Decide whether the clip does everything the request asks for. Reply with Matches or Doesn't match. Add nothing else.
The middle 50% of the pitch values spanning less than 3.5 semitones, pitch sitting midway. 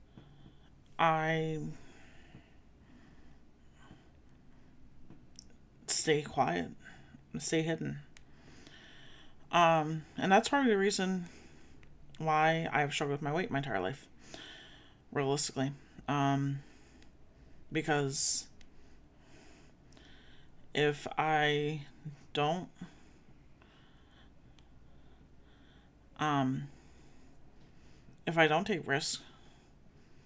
Matches